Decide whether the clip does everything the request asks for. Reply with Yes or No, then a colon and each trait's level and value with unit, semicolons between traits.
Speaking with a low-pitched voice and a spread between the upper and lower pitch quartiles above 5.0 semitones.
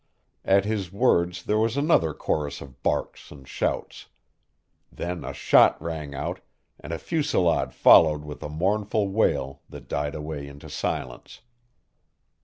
Yes: very low, 85 Hz; wide, 5.4 semitones